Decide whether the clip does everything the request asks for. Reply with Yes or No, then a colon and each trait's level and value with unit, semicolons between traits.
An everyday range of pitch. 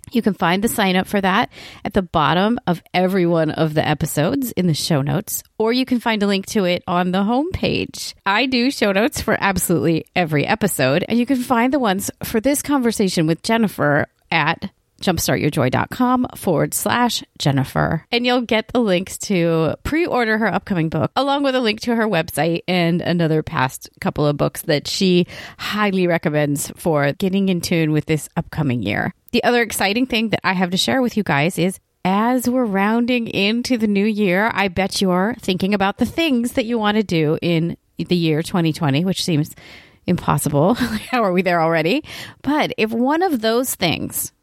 No: wide, 5.9 semitones